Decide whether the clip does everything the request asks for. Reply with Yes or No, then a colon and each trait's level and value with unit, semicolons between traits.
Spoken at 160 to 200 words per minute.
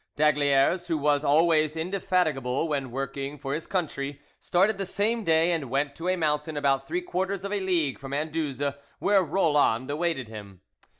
Yes: average, 170 wpm